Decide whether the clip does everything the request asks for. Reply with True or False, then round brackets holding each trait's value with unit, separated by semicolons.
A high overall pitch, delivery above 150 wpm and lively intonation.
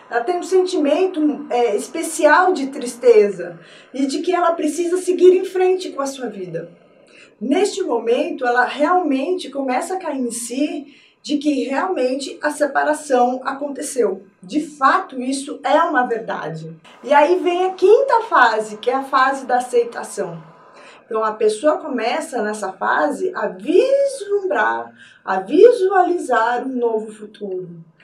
False (270 Hz; 140 wpm; 6.6 semitones)